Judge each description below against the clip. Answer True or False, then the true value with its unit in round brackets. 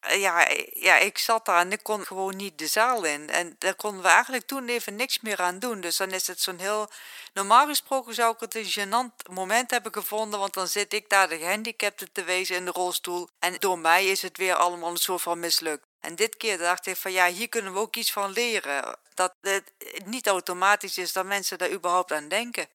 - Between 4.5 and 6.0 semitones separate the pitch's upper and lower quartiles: False (3.6 semitones)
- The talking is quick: True (230 wpm)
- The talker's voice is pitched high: True (195 Hz)